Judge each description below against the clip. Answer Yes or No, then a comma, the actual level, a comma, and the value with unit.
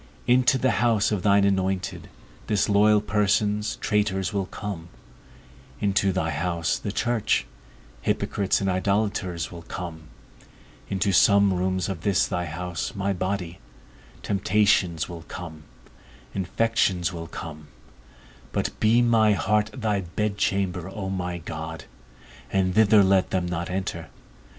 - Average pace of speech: No, slow, 125 wpm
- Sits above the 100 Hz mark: No, very low, 95 Hz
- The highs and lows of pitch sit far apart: No, average, 2.9 semitones